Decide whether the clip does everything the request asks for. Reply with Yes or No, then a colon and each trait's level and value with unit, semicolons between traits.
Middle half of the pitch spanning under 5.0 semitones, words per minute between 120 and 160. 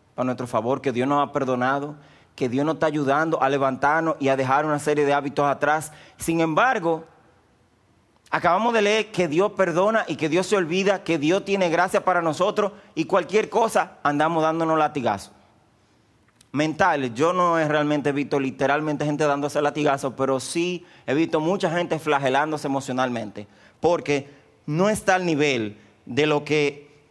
No: average, 3.8 semitones; average, 170 wpm